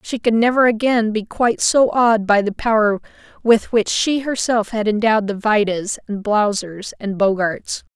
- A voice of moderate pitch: No, high, 215 Hz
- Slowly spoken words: No, average, 175 wpm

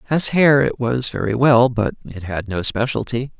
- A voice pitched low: Yes, low, 125 Hz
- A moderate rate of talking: Yes, average, 195 wpm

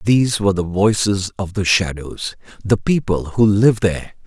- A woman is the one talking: No, male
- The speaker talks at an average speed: Yes, average, 170 wpm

